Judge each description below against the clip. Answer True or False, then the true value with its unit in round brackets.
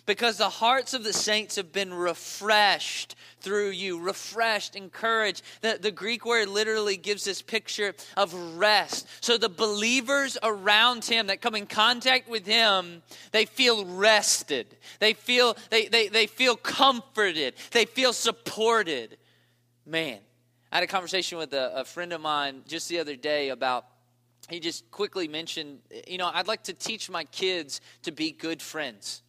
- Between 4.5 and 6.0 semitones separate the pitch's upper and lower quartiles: True (5.0 semitones)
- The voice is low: False (200 Hz)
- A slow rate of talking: False (160 wpm)